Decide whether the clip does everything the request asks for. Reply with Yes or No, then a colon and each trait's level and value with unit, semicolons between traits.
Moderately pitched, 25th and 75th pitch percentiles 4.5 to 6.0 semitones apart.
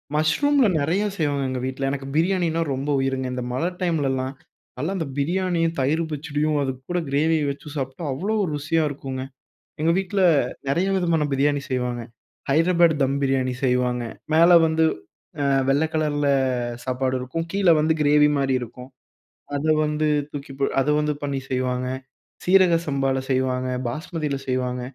No: medium, 145 Hz; average, 3.8 semitones